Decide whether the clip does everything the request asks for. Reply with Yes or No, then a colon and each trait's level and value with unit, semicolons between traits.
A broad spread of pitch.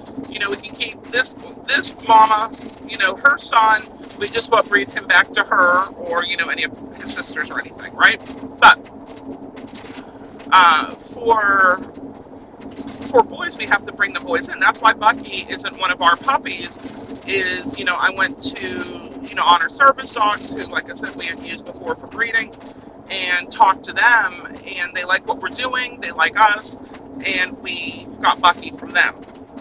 No: average, 3.9 semitones